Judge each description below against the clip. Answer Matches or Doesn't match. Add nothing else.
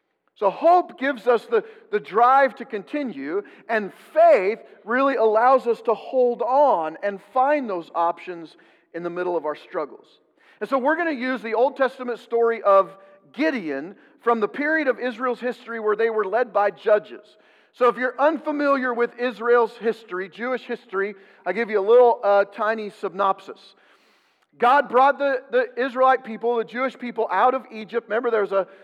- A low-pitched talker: Doesn't match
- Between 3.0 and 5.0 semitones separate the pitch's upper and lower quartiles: Matches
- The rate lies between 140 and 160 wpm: Doesn't match